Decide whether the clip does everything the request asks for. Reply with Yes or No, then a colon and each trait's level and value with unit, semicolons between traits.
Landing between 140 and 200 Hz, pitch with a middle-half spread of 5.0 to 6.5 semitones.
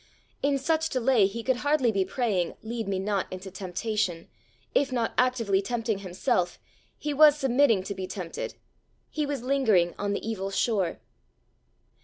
No: high, 220 Hz; average, 5.3 semitones